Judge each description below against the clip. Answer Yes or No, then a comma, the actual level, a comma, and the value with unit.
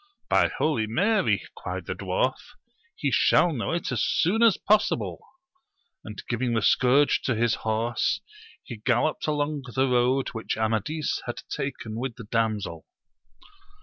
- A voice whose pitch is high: No, low, 125 Hz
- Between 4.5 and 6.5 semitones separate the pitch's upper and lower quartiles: Yes, average, 5.1 semitones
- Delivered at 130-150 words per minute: Yes, average, 145 wpm